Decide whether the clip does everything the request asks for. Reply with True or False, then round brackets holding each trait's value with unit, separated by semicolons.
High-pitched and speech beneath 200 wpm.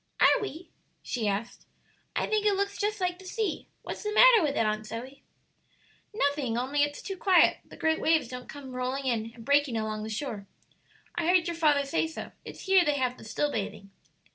False (285 Hz; 205 wpm)